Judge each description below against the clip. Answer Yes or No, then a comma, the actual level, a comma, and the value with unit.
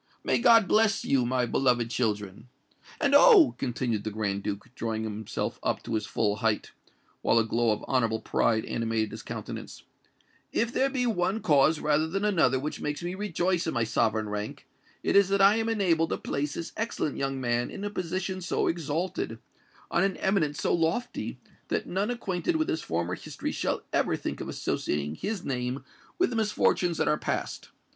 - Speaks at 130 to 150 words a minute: No, average, 180 wpm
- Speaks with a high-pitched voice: No, medium, 150 Hz